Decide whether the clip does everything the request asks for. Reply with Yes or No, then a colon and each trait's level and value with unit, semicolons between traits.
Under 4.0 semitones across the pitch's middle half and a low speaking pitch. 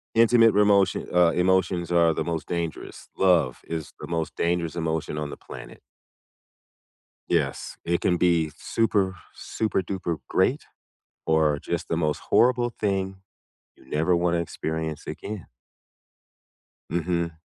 Yes: average, 2.8 semitones; very low, 85 Hz